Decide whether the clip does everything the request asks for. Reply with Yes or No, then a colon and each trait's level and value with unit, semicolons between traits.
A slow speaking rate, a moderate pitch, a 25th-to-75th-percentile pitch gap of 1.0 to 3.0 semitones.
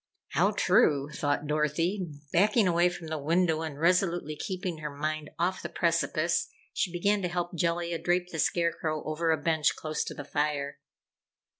No: average, 165 wpm; medium, 165 Hz; narrow, 2.5 semitones